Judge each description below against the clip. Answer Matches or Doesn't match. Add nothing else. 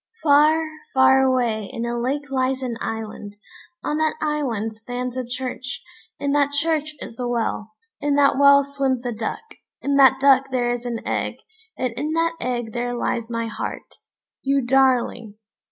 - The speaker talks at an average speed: Matches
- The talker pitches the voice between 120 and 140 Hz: Doesn't match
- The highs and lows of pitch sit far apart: Doesn't match